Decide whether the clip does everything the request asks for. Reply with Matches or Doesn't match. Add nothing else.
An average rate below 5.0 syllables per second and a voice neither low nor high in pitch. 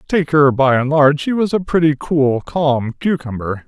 Matches